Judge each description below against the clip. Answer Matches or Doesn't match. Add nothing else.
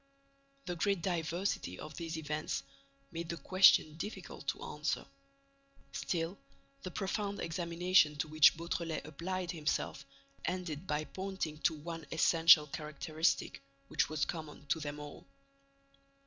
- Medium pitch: Matches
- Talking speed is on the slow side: Matches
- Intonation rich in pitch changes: Doesn't match